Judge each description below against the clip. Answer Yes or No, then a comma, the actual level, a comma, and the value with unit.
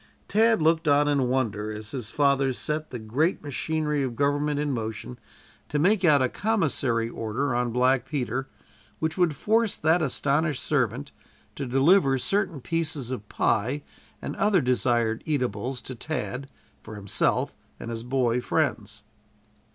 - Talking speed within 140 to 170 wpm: Yes, average, 150 wpm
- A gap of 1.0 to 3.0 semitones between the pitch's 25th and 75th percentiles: No, average, 4.2 semitones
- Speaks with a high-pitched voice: No, low, 135 Hz